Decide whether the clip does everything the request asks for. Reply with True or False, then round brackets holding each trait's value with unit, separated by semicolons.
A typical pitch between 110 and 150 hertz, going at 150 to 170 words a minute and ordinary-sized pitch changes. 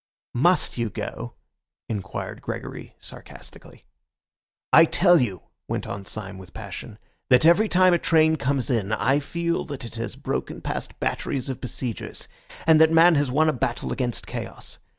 False (135 Hz; 160 wpm; 6.1 semitones)